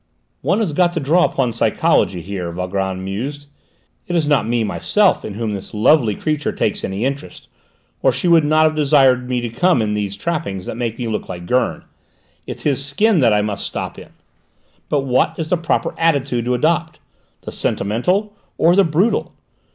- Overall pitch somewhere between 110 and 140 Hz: Yes, low, 135 Hz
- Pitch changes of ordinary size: No, wide, 7.1 semitones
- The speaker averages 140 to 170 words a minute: No, average, 190 wpm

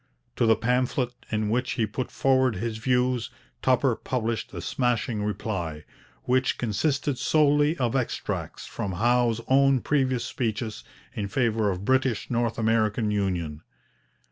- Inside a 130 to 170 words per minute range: Yes, slow, 135 wpm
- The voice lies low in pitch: Yes, low, 120 Hz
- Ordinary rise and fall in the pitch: Yes, average, 3.2 semitones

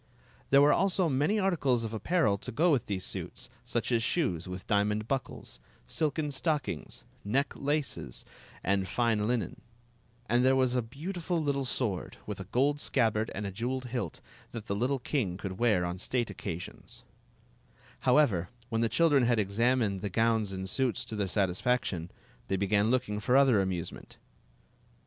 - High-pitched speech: No, low, 115 Hz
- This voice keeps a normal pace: Yes, average, 165 wpm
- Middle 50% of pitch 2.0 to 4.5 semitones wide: No, average, 5.3 semitones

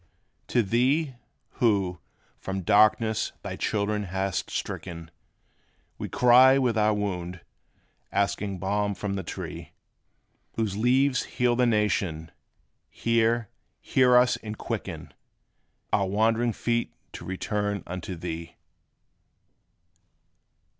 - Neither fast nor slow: No, slow, 105 wpm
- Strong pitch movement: No, average, 3.7 semitones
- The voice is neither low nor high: No, low, 105 Hz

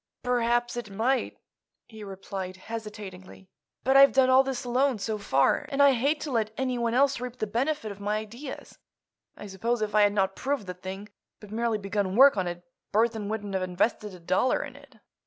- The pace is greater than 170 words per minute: Yes, average, 195 wpm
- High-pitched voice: Yes, high, 220 Hz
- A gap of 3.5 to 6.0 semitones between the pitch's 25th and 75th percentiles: Yes, average, 4.0 semitones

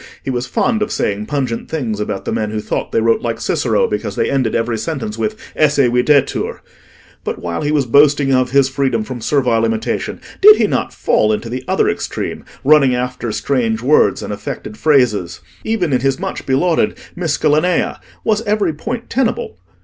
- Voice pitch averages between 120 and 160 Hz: Yes, low, 135 Hz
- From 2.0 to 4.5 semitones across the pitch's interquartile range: No, average, 5.1 semitones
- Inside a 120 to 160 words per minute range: No, average, 180 wpm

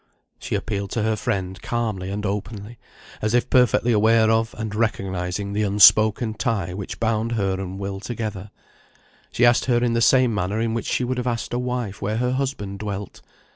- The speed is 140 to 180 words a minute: No, average, 190 wpm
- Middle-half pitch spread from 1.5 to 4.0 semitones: Yes, average, 2.8 semitones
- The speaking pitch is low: Yes, low, 110 Hz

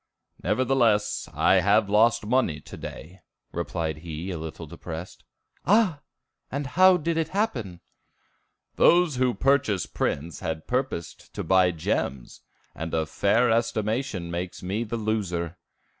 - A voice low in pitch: Yes, low, 105 Hz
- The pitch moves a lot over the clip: Yes, wide, 7.2 semitones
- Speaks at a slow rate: Yes, slow, 130 wpm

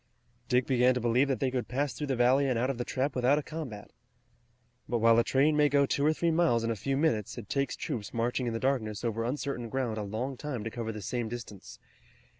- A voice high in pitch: No, low, 125 Hz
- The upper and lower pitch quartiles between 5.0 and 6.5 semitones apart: No, average, 3.2 semitones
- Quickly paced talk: Yes, fast, 245 wpm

